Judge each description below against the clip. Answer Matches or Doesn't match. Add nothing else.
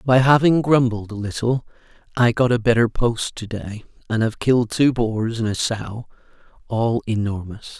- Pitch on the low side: Matches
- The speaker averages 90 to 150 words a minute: Doesn't match